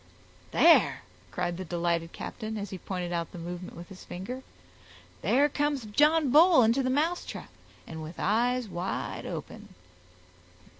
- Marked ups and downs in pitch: Yes, wide, 7.3 semitones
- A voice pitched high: Yes, high, 210 Hz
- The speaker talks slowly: No, average, 145 wpm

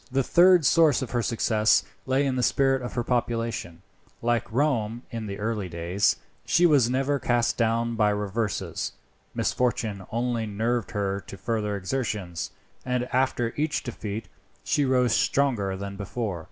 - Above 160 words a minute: No, average, 155 wpm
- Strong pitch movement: No, average, 3.7 semitones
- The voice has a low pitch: Yes, low, 115 Hz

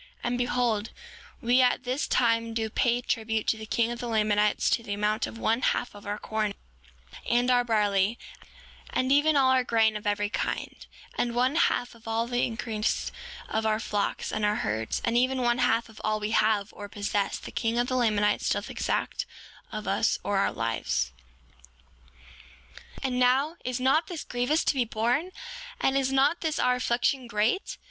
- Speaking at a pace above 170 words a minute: Yes, average, 185 wpm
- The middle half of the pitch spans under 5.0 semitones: Yes, average, 2.8 semitones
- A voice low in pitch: No, high, 235 Hz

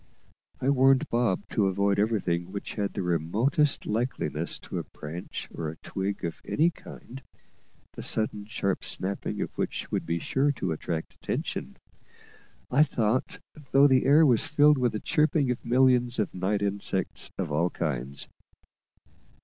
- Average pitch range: No, wide, 6.1 semitones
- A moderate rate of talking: Yes, average, 150 wpm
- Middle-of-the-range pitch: No, low, 105 Hz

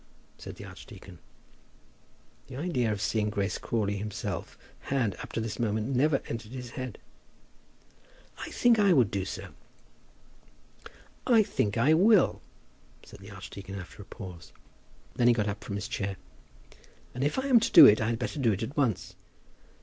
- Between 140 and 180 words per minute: Yes, average, 165 wpm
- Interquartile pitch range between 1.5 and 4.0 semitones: No, average, 5.3 semitones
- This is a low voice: Yes, low, 115 Hz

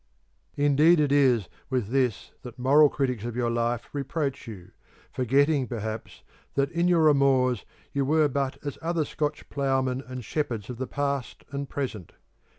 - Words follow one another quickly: No, average, 155 wpm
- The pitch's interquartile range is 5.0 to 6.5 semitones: No, average, 2.8 semitones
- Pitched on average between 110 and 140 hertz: Yes, low, 135 Hz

